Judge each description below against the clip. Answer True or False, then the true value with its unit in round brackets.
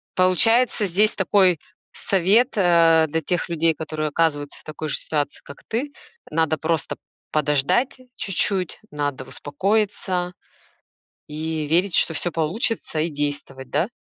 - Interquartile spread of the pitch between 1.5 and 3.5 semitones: False (4.0 semitones)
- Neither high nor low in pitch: True (165 Hz)